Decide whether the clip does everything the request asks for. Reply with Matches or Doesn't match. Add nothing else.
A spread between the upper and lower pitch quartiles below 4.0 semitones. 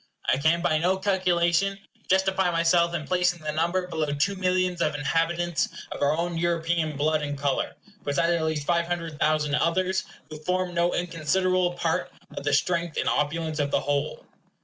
Matches